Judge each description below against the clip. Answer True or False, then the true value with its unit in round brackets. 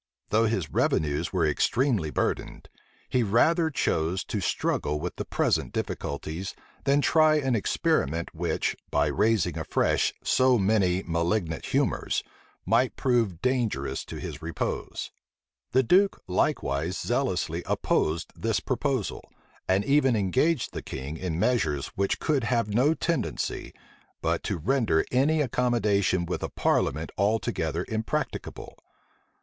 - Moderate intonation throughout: False (7.3 semitones)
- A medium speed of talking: False (125 wpm)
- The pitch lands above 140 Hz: False (105 Hz)